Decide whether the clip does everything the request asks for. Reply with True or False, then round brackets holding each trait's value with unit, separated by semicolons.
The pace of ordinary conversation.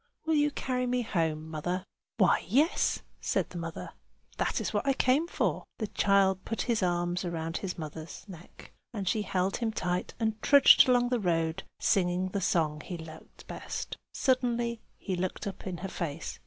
True (180 wpm)